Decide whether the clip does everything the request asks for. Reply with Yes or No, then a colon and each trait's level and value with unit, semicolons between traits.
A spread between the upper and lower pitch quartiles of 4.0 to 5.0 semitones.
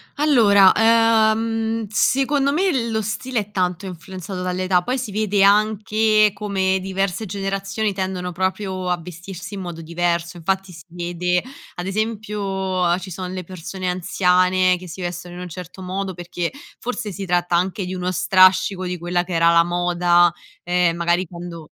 No: average, 2.8 semitones